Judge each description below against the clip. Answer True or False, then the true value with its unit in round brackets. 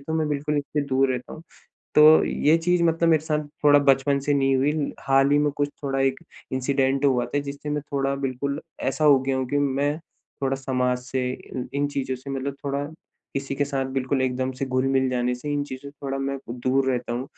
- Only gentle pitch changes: True (1.6 semitones)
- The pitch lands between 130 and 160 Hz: True (135 Hz)